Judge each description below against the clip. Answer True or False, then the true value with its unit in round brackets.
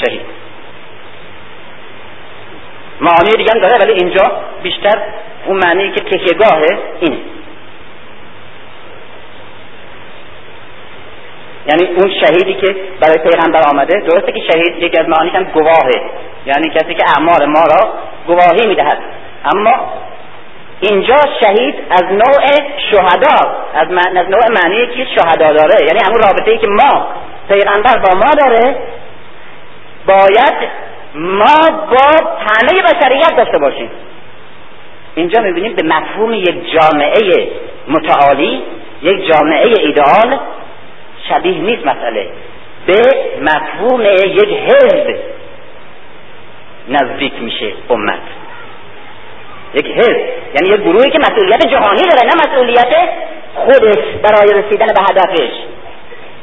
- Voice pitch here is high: True (260 Hz)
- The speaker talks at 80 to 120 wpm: True (105 wpm)